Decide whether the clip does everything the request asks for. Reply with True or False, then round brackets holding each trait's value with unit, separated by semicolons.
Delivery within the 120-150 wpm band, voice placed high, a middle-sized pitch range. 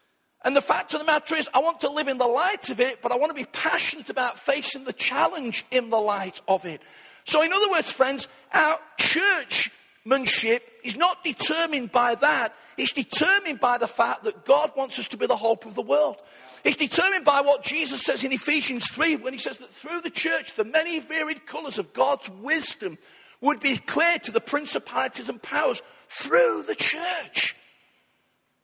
False (195 wpm; 280 Hz; 4.2 semitones)